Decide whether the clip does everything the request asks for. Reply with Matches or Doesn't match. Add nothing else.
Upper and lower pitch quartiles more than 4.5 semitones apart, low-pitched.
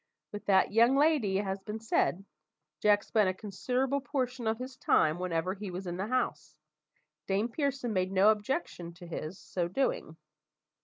Doesn't match